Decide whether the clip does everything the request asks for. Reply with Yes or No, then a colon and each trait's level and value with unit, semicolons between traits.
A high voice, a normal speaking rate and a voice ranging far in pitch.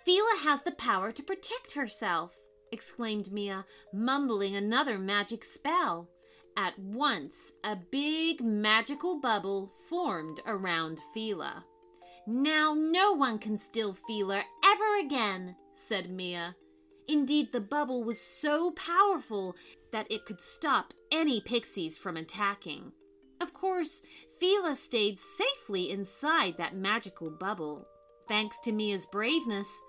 No: high, 215 Hz; slow, 120 wpm; wide, 7.7 semitones